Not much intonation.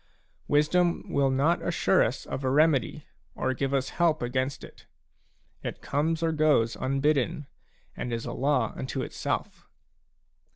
No: average, 3.0 semitones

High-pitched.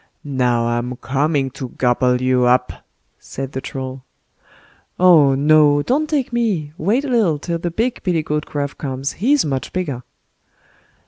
No: medium, 145 Hz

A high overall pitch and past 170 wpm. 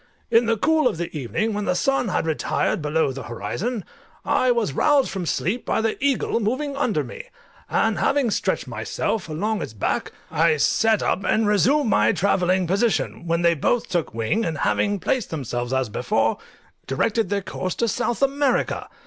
Yes: high, 200 Hz; average, 180 wpm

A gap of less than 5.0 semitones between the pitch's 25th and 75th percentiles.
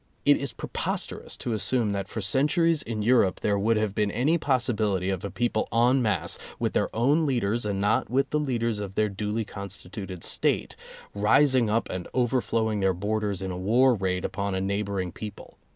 Yes: average, 3.7 semitones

